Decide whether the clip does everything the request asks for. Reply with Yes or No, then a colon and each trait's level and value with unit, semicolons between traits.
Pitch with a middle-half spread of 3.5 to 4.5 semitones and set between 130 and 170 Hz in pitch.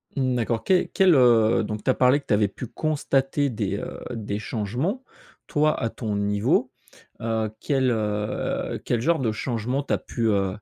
No: average, 4.2 semitones; low, 120 Hz